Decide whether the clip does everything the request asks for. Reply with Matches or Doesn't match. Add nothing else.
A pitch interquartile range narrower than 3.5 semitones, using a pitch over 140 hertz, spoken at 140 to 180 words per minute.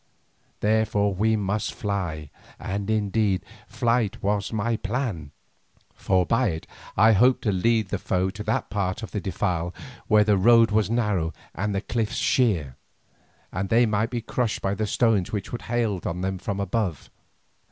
Doesn't match